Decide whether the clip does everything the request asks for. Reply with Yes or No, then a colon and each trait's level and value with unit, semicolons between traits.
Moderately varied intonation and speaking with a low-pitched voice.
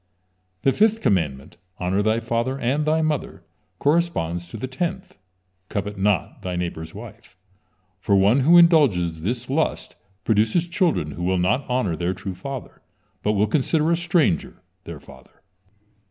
No: wide, 8.7 semitones; low, 110 Hz